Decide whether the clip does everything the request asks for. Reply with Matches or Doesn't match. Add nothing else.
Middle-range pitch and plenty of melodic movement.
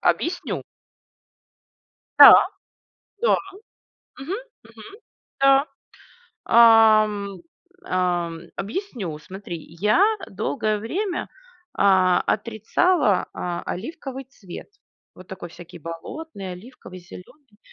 Doesn't match